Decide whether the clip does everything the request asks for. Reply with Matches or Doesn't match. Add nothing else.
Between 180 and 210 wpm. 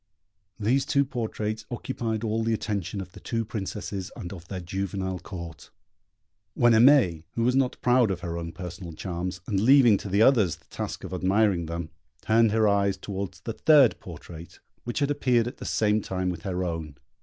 Matches